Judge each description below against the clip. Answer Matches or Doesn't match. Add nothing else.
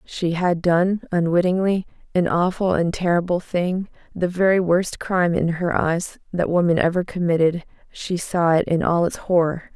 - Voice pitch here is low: Doesn't match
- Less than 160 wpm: Matches